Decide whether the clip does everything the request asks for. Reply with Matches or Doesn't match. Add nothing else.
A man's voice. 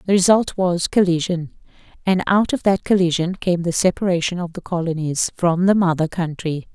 Doesn't match